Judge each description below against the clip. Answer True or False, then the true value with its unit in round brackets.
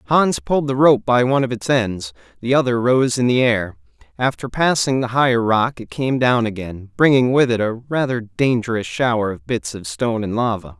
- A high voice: False (120 Hz)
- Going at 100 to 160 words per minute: False (205 wpm)